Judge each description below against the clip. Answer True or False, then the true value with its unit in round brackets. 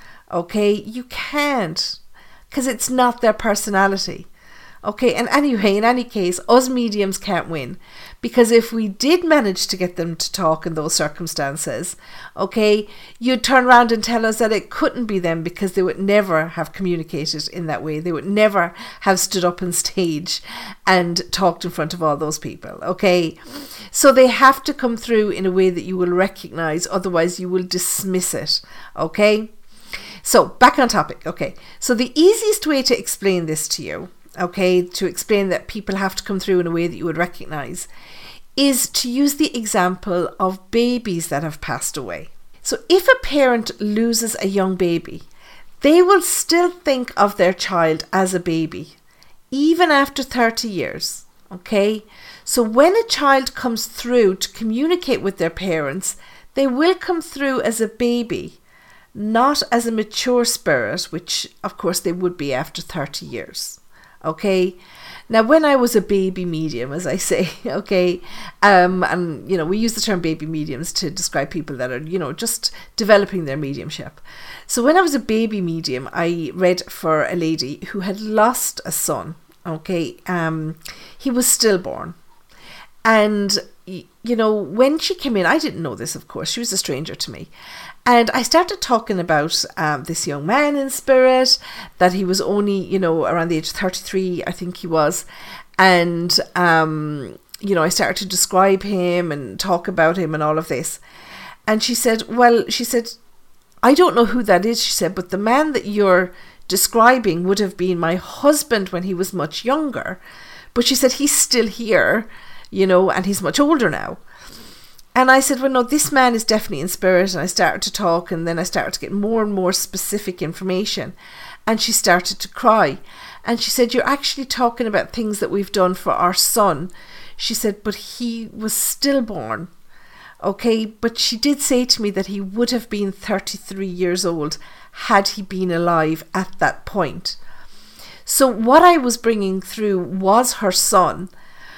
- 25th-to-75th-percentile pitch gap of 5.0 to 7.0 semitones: True (5.3 semitones)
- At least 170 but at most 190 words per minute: True (180 wpm)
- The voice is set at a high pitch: True (200 Hz)